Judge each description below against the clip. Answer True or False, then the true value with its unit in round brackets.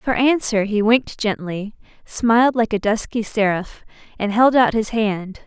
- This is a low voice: False (220 Hz)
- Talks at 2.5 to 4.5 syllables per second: True (4.4 syllables/s)